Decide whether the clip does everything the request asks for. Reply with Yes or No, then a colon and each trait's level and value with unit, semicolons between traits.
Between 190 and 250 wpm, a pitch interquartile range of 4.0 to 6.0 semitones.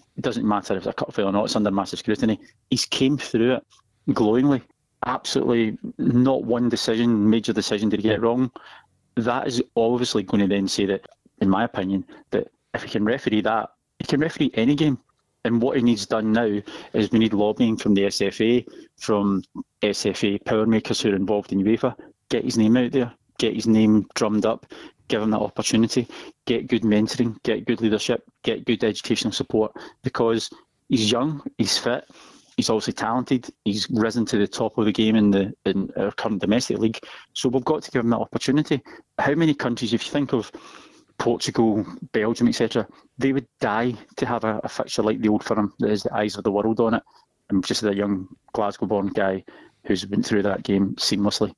No: average, 200 wpm; narrow, 2.5 semitones